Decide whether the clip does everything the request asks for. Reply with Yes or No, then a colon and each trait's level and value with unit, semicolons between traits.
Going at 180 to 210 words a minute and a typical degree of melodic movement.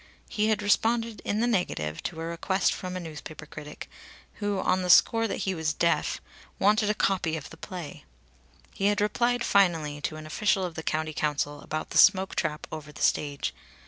Yes: average, 195 wpm; average, 4.8 semitones